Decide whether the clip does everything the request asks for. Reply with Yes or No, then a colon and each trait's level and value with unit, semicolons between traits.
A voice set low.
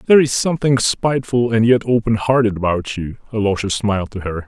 Yes: low, 110 Hz